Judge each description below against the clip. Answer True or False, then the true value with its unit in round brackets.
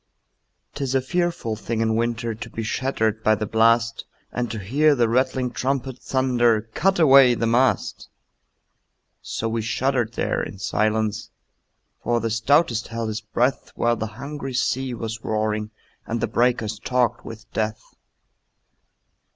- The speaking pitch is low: True (115 Hz)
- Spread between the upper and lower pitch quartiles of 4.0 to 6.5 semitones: False (2.8 semitones)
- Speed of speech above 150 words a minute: False (145 wpm)